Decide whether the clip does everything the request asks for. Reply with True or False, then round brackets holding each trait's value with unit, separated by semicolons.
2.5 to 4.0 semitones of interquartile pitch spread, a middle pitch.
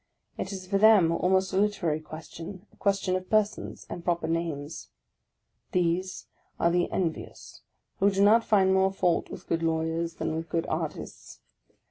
True (2.8 semitones; 180 Hz)